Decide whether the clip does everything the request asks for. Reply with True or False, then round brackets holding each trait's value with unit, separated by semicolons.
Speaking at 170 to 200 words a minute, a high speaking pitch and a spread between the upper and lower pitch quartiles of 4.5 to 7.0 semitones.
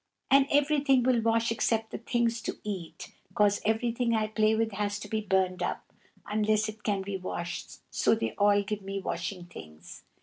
False (180 wpm; 215 Hz; 2.7 semitones)